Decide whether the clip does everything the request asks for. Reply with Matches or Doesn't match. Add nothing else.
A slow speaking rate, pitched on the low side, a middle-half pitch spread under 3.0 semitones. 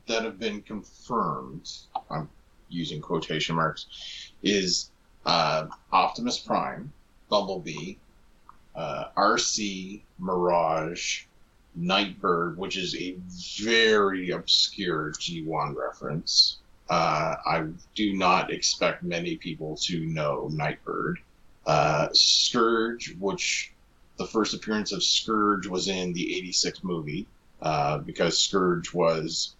Doesn't match